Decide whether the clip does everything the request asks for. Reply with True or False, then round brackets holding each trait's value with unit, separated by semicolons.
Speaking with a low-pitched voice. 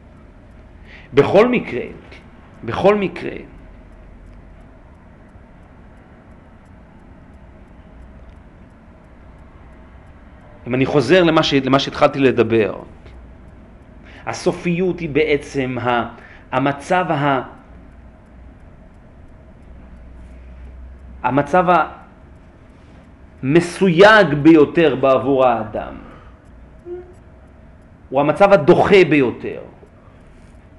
True (95 Hz)